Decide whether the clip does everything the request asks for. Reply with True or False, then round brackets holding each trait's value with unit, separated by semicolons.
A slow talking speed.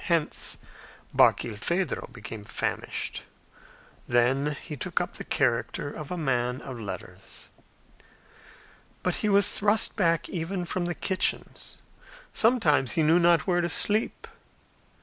True (125 wpm)